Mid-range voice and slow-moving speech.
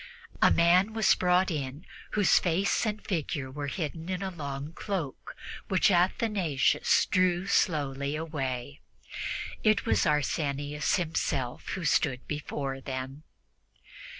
Yes: medium, 155 Hz; slow, 120 wpm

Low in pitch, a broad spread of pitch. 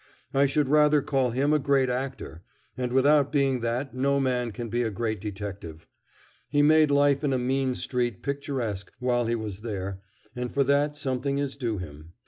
No: low, 130 Hz; average, 3.5 semitones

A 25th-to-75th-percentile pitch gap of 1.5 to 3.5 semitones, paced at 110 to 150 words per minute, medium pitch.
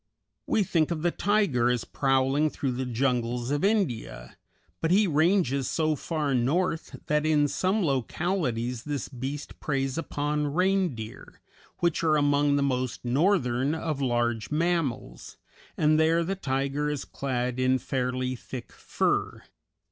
No: average, 4.2 semitones; average, 140 wpm; medium, 145 Hz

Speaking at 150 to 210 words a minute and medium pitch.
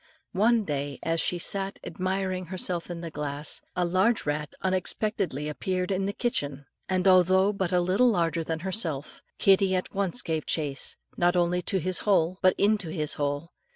Yes: average, 170 wpm; medium, 180 Hz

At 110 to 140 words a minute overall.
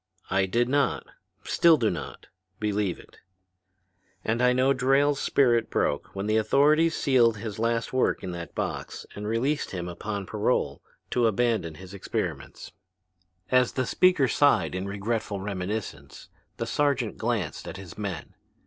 No: average, 150 wpm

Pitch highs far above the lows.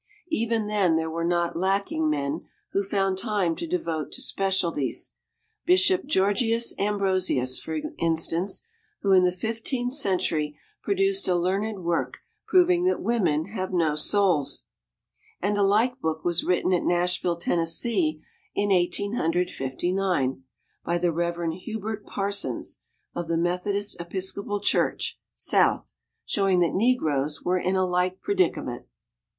No: average, 3.3 semitones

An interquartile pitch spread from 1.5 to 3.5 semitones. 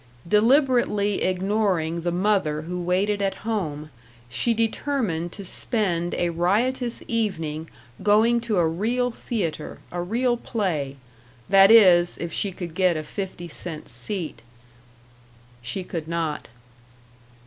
No: average, 4.6 semitones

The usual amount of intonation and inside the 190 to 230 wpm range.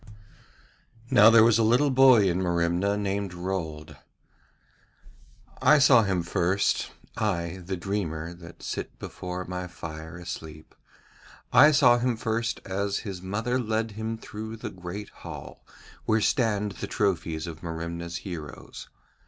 No: average, 4.5 semitones; slow, 135 wpm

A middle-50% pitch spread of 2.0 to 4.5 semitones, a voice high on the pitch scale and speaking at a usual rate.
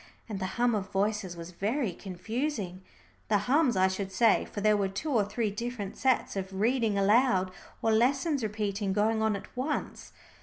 Yes: average, 3.7 semitones; high, 210 Hz; average, 180 wpm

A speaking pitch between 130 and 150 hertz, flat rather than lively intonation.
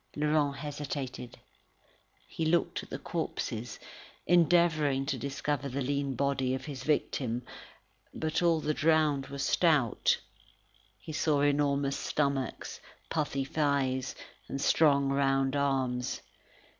Yes: medium, 140 Hz; narrow, 2.0 semitones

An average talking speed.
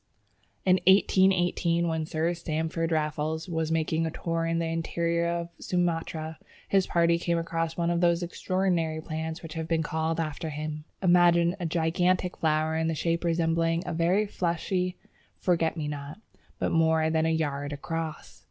Yes: average, 160 wpm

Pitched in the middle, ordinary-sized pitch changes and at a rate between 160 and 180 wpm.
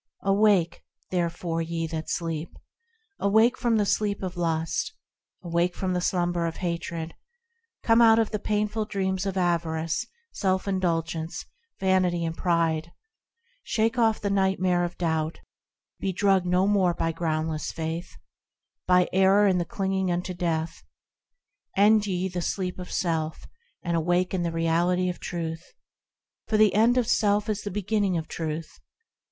No: medium, 180 Hz; average, 3.0 semitones; average, 150 wpm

